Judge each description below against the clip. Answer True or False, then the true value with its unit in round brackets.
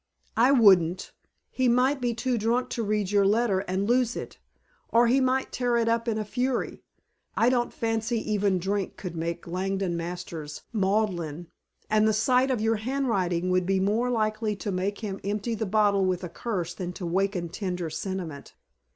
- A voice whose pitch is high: True (205 Hz)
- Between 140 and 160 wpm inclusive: False (180 wpm)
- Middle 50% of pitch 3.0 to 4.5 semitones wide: True (4.2 semitones)